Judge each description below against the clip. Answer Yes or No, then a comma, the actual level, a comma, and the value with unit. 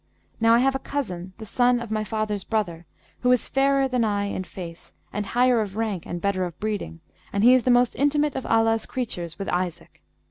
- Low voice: No, high, 220 Hz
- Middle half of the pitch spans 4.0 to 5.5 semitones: Yes, average, 4.4 semitones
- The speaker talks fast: Yes, fast, 215 wpm